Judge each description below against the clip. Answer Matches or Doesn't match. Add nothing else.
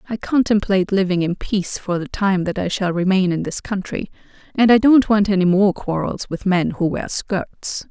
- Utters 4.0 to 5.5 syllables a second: Matches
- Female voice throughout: Matches